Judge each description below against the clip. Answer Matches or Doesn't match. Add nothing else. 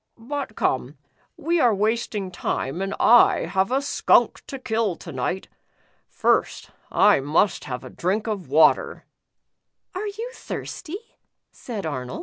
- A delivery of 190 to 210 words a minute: Doesn't match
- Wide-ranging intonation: Matches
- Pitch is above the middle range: Matches